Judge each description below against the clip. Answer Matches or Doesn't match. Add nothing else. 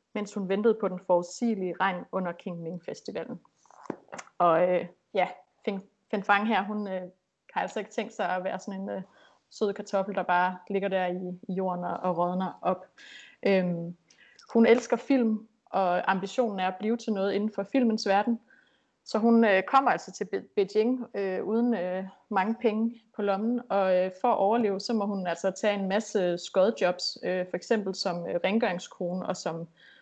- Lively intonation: Doesn't match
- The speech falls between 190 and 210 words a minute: Doesn't match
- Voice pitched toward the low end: Doesn't match